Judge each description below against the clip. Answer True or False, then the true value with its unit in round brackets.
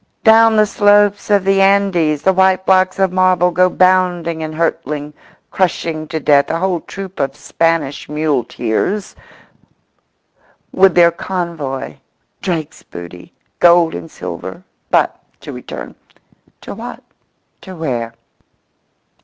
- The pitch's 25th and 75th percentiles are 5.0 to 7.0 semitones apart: False (3.7 semitones)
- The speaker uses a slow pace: True (115 wpm)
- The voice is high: False (175 Hz)